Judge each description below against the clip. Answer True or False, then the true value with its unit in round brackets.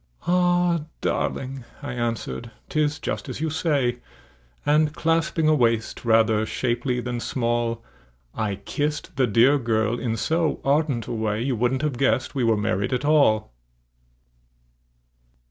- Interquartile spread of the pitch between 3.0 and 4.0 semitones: False (4.5 semitones)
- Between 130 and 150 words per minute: True (140 wpm)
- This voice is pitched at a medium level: False (125 Hz)